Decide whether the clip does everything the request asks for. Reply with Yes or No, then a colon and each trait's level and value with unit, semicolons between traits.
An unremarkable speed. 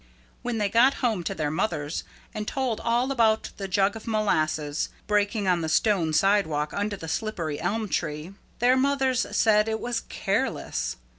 Yes: average, 165 wpm